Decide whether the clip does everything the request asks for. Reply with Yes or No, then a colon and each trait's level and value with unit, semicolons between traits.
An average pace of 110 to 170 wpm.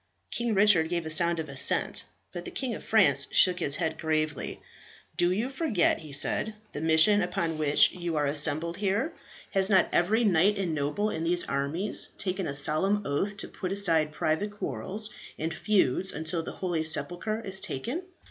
No: average, 180 wpm